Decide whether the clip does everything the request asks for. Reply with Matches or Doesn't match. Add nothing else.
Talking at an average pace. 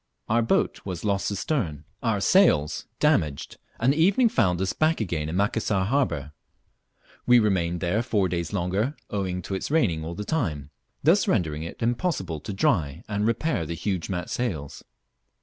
Matches